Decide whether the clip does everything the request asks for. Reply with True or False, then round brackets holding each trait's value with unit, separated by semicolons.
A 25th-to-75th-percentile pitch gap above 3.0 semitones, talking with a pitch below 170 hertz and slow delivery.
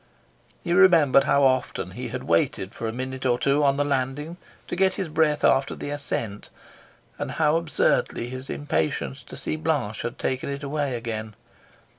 False (3.5 semitones; 140 Hz; 175 wpm)